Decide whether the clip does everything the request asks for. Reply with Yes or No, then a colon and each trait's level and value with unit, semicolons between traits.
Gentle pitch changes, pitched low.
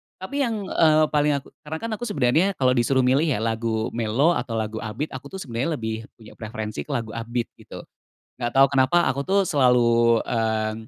No: average, 5.1 semitones; low, 125 Hz